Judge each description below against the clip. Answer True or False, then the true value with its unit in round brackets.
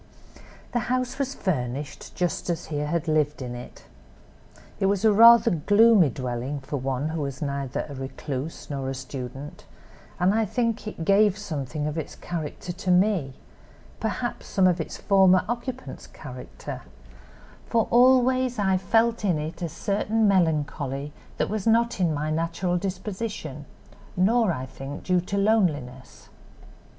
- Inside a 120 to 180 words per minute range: True (145 wpm)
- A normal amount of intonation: False (6.6 semitones)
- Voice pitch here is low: False (175 Hz)